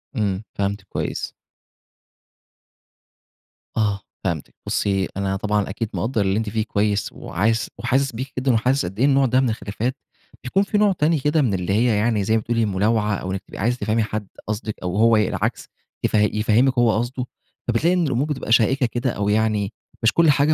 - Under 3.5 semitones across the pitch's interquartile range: No, average, 3.8 semitones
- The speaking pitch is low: Yes, low, 110 Hz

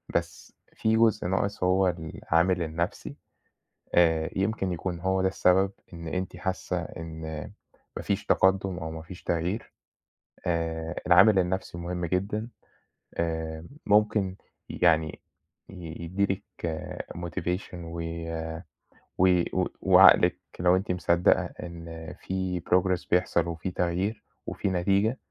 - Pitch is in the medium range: No, very low, 90 Hz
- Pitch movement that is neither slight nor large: No, narrow, 2.2 semitones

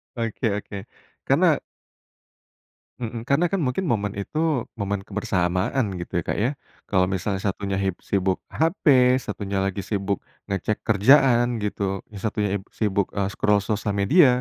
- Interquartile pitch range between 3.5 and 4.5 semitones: No, average, 3.1 semitones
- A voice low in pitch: Yes, low, 100 Hz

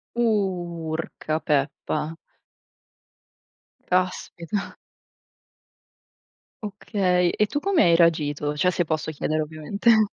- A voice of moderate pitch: Yes, medium, 175 Hz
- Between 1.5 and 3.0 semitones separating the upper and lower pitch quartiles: No, average, 4.3 semitones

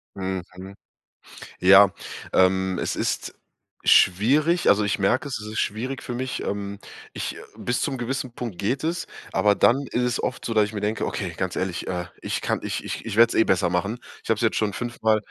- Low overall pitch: Yes, low, 105 Hz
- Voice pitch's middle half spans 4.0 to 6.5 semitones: Yes, average, 4.3 semitones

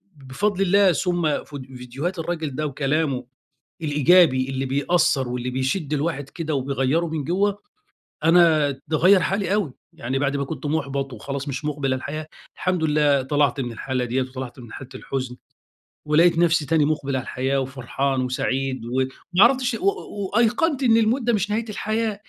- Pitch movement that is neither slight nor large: Yes, average, 4.9 semitones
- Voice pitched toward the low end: No, medium, 150 Hz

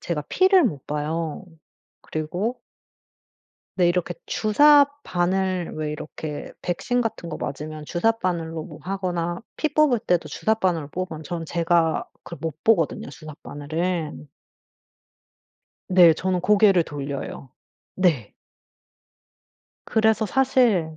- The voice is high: No, medium, 175 Hz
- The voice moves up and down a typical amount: Yes, average, 5.0 semitones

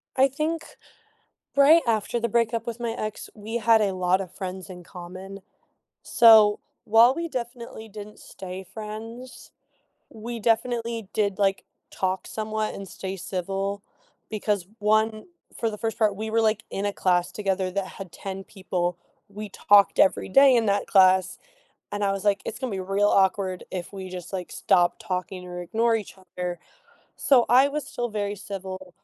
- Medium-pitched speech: No, high, 205 Hz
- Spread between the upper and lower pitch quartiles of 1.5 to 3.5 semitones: Yes, average, 3.2 semitones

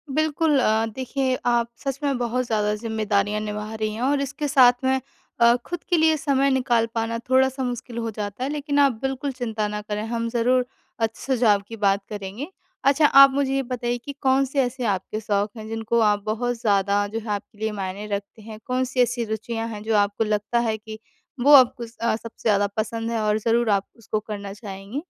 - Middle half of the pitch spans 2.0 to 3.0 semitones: No, average, 3.6 semitones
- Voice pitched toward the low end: No, high, 230 Hz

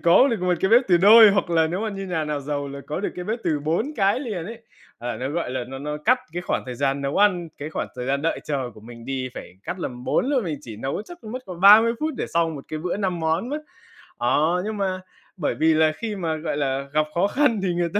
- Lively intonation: Yes, wide, 6.1 semitones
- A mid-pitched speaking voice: Yes, medium, 170 Hz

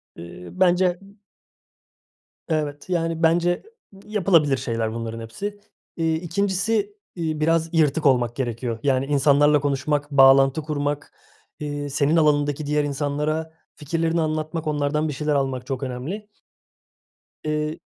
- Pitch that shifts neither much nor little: Yes, average, 3.0 semitones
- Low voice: No, medium, 150 Hz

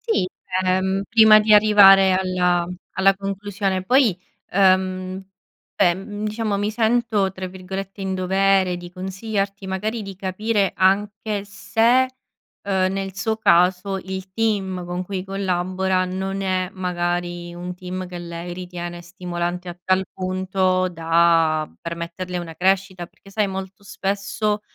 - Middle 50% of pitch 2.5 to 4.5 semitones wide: No, narrow, 1.7 semitones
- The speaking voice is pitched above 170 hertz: Yes, high, 190 Hz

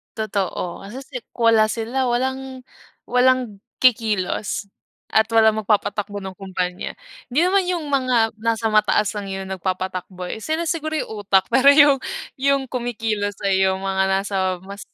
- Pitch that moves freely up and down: No, average, 4.8 semitones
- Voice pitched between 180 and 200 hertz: No, high, 220 Hz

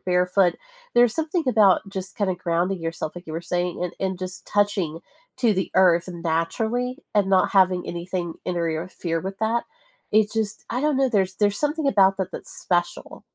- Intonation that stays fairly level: No, average, 3.5 semitones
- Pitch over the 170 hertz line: Yes, high, 190 Hz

